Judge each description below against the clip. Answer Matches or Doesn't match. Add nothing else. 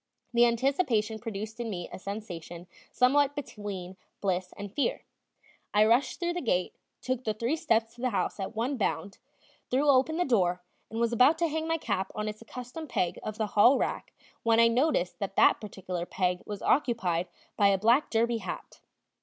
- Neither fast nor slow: Matches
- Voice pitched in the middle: Doesn't match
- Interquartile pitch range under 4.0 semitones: Doesn't match